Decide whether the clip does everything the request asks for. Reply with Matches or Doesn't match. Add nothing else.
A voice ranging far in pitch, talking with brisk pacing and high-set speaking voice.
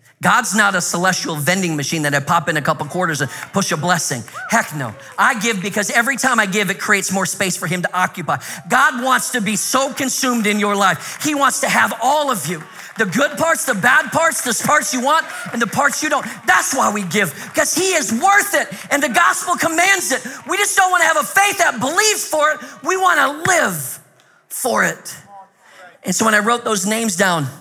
Matches